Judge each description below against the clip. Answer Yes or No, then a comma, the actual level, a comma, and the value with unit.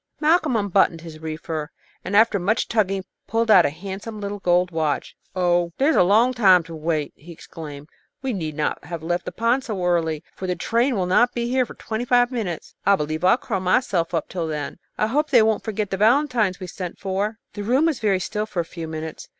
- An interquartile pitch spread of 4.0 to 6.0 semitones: Yes, average, 5.2 semitones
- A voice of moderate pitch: No, high, 195 Hz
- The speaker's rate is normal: No, fast, 225 wpm